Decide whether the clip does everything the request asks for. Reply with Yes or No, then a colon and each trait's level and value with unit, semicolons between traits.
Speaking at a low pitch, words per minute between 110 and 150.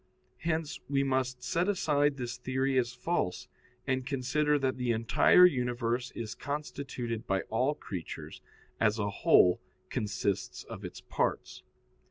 Yes: low, 130 Hz; slow, 135 wpm